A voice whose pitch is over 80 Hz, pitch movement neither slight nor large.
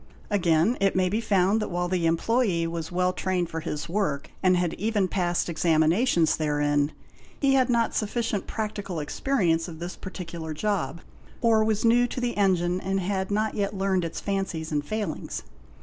Yes: medium, 185 Hz; average, 4.2 semitones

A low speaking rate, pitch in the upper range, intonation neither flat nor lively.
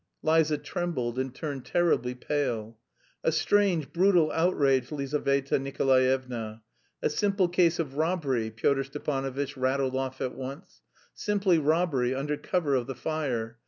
No: slow, 130 wpm; medium, 140 Hz; average, 3.8 semitones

